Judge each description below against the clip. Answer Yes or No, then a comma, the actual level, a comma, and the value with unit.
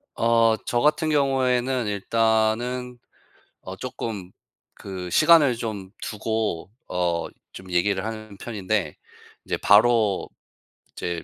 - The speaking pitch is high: No, low, 110 Hz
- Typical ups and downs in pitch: Yes, average, 4.1 semitones